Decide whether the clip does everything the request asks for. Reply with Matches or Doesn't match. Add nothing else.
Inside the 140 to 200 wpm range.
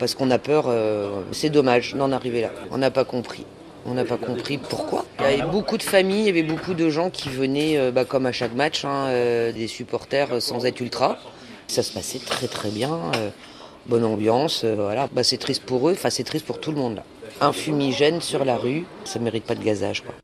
Doesn't match